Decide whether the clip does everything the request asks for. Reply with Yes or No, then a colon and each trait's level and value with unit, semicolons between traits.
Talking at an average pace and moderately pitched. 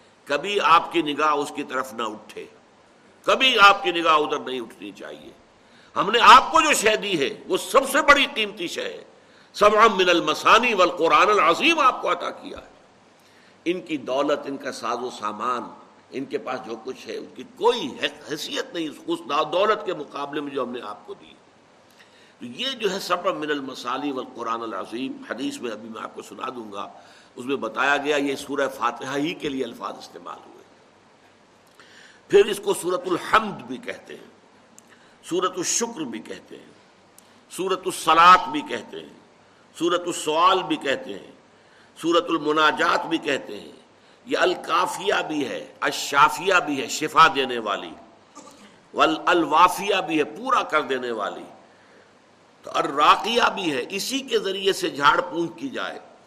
Yes: average, 175 wpm; medium, 175 Hz